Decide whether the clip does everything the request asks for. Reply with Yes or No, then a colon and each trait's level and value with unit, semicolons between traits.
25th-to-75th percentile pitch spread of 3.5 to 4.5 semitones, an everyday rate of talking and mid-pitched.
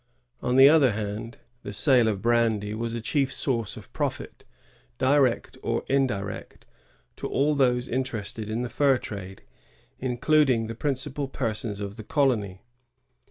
No: average, 3.8 semitones; average, 145 wpm; low, 120 Hz